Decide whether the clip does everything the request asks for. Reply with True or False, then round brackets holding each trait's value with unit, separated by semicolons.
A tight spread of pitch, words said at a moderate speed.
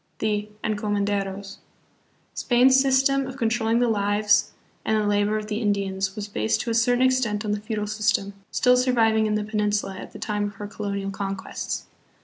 True (2.0 semitones; 180 wpm)